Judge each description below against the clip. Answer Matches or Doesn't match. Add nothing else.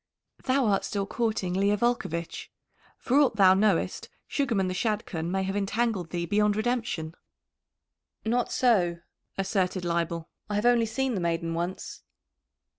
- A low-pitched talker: Doesn't match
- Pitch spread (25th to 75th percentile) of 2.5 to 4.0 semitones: Doesn't match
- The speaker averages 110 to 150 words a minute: Matches